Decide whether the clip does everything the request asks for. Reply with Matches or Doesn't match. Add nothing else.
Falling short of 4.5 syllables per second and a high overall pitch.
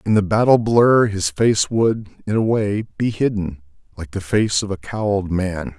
Doesn't match